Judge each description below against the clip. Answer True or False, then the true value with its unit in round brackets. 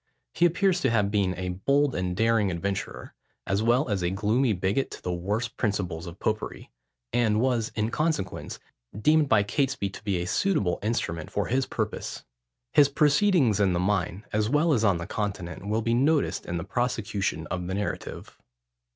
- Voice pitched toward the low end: True (105 Hz)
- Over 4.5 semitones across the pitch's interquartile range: True (5.2 semitones)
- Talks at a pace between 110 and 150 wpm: False (180 wpm)